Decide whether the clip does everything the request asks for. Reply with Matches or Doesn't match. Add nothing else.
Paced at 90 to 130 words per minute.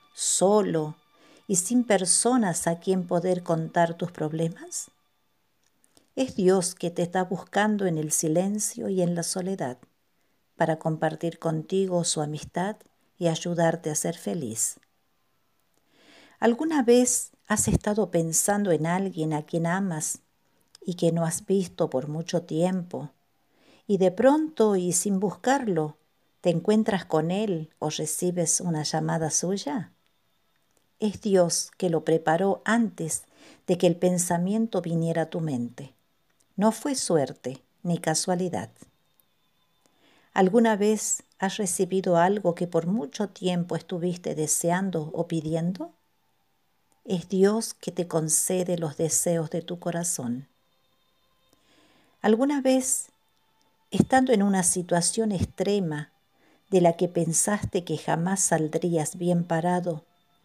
Matches